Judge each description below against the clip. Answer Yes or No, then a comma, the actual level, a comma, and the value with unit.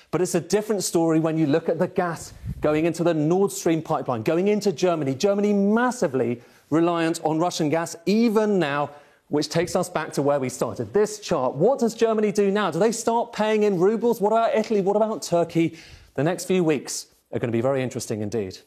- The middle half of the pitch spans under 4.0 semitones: No, average, 4.8 semitones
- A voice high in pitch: No, medium, 175 Hz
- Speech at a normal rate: No, fast, 210 wpm